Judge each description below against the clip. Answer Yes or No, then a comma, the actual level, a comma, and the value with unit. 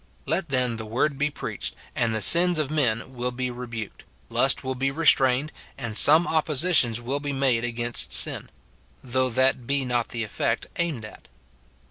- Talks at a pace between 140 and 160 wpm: No, average, 170 wpm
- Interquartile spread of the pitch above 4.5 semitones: No, average, 3.4 semitones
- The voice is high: No, low, 130 Hz